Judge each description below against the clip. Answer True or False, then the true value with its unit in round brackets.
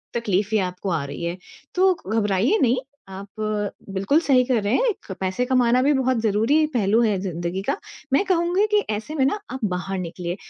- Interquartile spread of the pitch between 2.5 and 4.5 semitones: False (5.5 semitones)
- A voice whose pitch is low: False (220 Hz)